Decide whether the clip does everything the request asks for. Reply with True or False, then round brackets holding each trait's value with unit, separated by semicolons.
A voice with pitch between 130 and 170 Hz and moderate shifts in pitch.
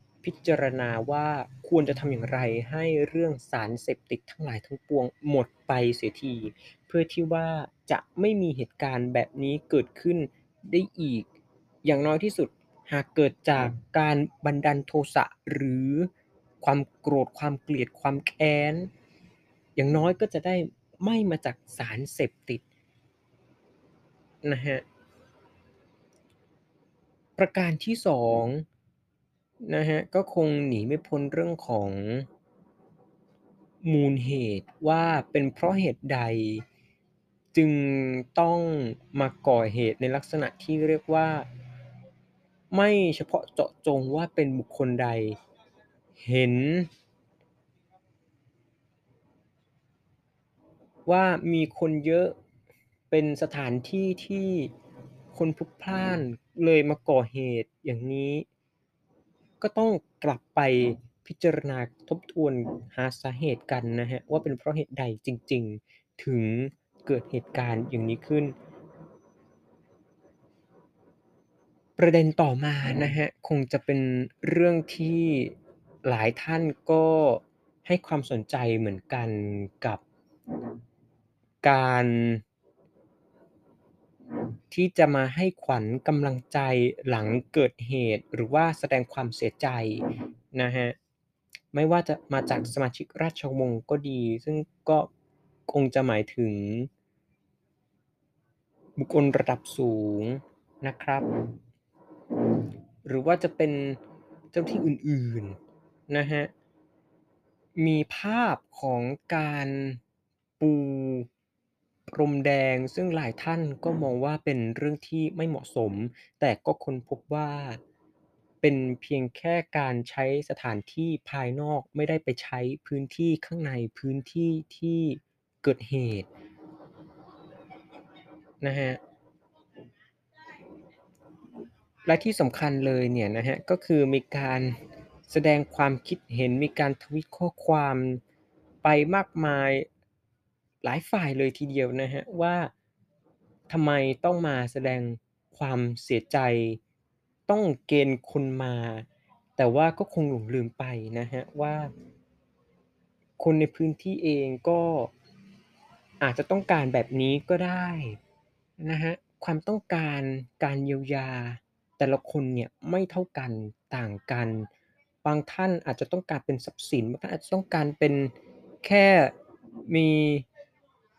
True (140 Hz; 4.2 semitones)